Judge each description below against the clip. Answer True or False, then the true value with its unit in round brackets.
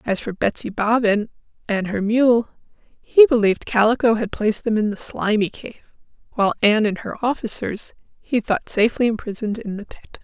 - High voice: True (220 Hz)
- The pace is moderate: True (170 wpm)